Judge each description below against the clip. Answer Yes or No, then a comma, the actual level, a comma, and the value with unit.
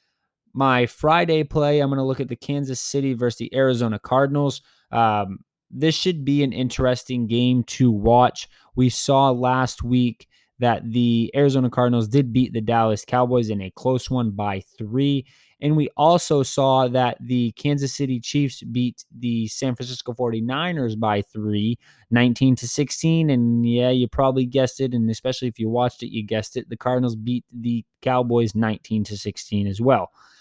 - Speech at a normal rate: Yes, average, 170 wpm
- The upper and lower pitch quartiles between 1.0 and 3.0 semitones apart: Yes, narrow, 2.5 semitones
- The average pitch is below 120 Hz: No, low, 125 Hz